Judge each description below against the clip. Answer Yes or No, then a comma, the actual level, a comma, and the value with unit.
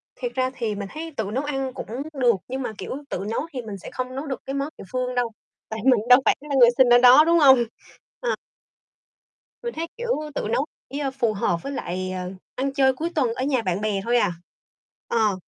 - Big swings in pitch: No, average, 3.7 semitones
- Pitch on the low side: No, very high, 255 Hz